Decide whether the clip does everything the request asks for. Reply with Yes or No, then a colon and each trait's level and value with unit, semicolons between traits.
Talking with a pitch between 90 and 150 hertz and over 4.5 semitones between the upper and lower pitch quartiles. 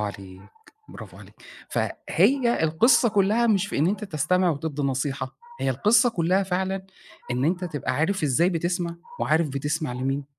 No: medium, 170 Hz; average, 5.2 semitones